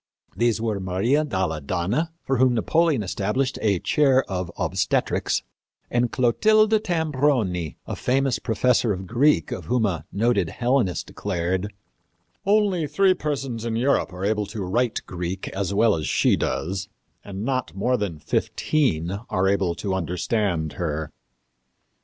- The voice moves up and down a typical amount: No, wide, 5.9 semitones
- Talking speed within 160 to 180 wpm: No, average, 140 wpm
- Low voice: Yes, low, 110 Hz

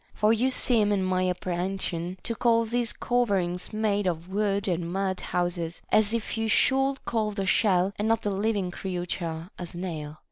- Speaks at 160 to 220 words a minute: Yes, average, 180 wpm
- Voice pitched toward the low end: No, high, 195 Hz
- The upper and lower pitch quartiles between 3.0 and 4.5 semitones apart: Yes, average, 3.6 semitones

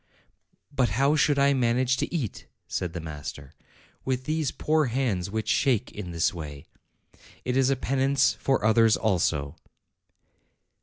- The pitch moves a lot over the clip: Yes, wide, 6.9 semitones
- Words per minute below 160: Yes, average, 145 wpm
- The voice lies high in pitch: No, low, 125 Hz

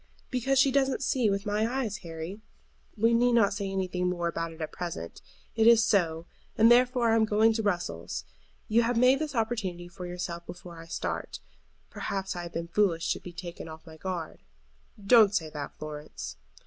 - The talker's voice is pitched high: Yes, high, 195 Hz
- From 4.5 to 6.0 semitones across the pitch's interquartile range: Yes, average, 5.1 semitones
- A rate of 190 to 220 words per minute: Yes, average, 195 wpm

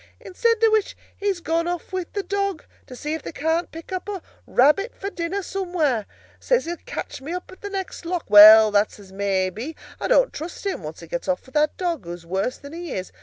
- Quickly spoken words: Yes, fast, 225 wpm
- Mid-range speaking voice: No, very high, 330 Hz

